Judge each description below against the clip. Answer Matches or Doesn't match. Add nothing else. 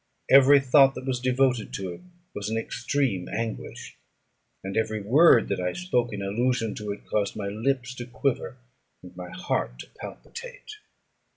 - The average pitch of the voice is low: Matches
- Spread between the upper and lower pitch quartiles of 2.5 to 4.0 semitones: Doesn't match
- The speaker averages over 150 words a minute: Matches